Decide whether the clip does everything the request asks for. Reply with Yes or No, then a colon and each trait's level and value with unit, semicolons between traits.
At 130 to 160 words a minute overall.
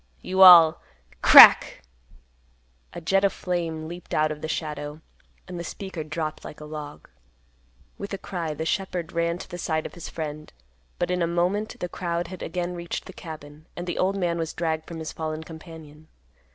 No: average, 190 wpm